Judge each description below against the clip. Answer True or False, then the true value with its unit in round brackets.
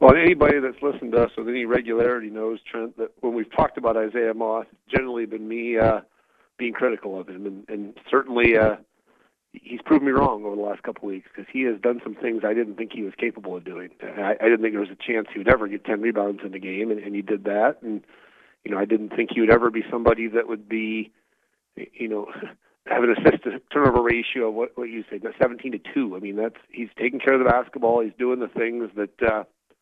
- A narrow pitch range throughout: True (2.1 semitones)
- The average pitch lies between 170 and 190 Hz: False (115 Hz)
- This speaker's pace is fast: True (240 wpm)